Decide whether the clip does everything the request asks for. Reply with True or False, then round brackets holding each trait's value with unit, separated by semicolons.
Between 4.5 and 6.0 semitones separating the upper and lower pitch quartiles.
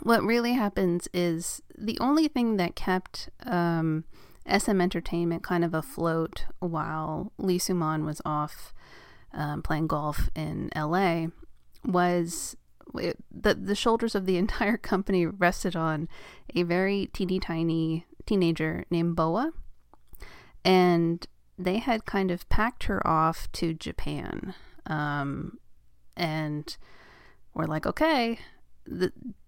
False (3.4 semitones)